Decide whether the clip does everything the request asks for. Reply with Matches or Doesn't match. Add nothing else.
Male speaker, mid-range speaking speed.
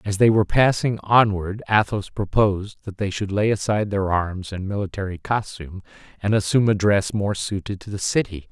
Matches